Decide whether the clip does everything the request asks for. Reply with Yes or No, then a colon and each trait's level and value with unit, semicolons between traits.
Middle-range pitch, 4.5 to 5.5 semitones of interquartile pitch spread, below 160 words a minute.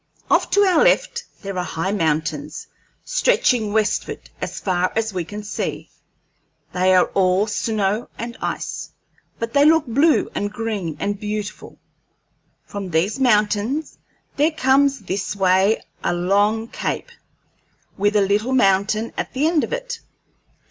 No: high, 210 Hz; average, 4.9 semitones; average, 140 wpm